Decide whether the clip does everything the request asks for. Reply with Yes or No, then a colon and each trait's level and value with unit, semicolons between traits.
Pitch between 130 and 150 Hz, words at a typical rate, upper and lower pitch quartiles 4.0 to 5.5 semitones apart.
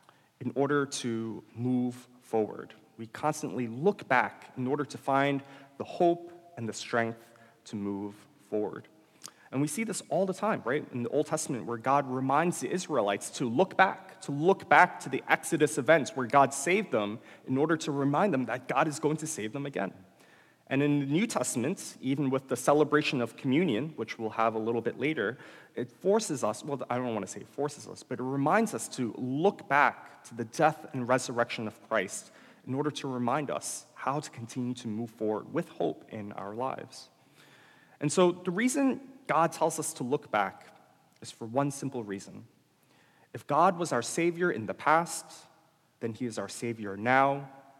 Yes: low, 135 Hz; average, 195 wpm; average, 4.7 semitones